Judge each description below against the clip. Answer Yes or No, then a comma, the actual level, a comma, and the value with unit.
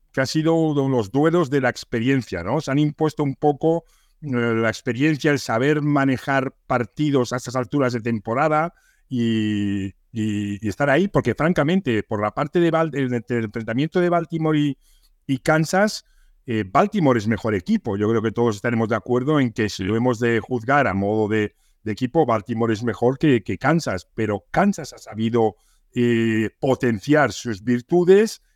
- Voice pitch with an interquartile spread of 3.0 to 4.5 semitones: No, average, 4.9 semitones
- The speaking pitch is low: Yes, low, 125 Hz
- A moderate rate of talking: Yes, average, 180 wpm